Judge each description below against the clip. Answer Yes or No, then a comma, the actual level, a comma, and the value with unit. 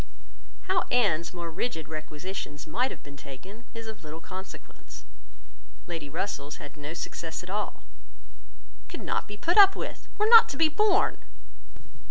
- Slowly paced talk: No, average, 155 wpm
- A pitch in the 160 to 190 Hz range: Yes, medium, 185 Hz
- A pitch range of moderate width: No, wide, 7.9 semitones